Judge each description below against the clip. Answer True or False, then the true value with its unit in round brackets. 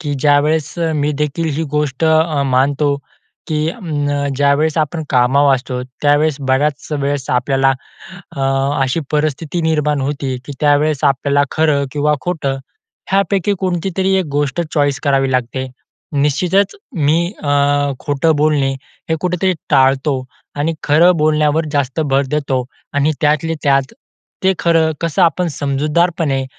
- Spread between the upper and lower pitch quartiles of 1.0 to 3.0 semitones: True (2.6 semitones)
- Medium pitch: True (150 Hz)